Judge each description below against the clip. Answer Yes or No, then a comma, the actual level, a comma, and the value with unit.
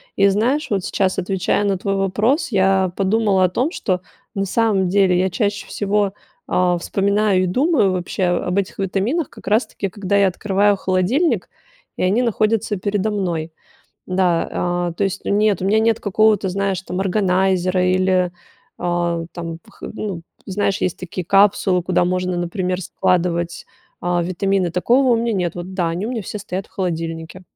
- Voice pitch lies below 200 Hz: Yes, high, 190 Hz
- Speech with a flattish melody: Yes, narrow, 2.2 semitones